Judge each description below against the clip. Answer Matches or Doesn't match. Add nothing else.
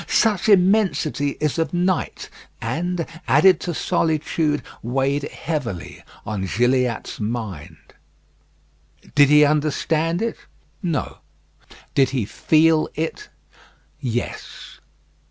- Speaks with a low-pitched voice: Doesn't match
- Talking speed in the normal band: Doesn't match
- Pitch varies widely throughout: Doesn't match